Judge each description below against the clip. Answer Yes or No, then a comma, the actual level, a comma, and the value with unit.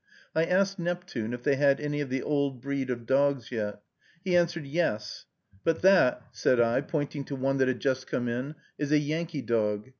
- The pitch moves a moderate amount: Yes, average, 4.0 semitones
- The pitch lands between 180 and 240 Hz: No, medium, 140 Hz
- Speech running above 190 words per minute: Yes, average, 200 wpm